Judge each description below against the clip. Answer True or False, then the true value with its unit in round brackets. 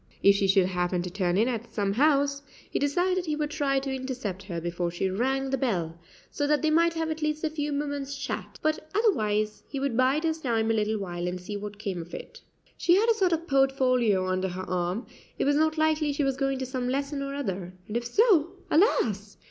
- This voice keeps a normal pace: False (230 wpm)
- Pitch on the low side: False (260 Hz)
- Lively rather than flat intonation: True (7.1 semitones)